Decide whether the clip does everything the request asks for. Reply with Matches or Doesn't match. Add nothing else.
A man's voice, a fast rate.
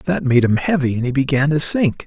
Matches